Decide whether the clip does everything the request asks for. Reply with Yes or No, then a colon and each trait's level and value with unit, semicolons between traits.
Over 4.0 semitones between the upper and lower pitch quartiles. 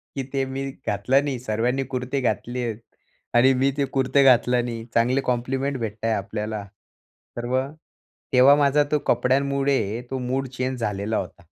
No: average, 2.7 semitones